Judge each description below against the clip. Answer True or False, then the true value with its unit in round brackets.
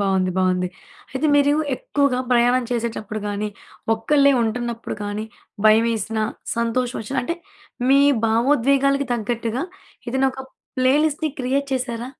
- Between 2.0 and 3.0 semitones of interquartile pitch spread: False (3.7 semitones)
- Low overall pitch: False (245 Hz)